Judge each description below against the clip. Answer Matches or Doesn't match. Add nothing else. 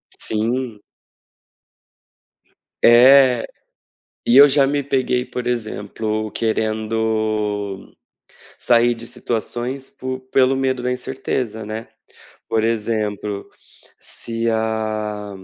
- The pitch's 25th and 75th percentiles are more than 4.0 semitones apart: Doesn't match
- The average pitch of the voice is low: Matches